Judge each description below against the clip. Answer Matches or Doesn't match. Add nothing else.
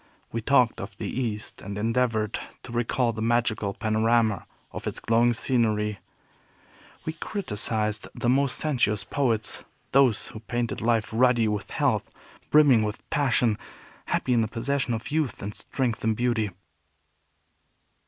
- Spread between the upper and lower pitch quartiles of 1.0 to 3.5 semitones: Matches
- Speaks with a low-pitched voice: Matches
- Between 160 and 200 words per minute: Doesn't match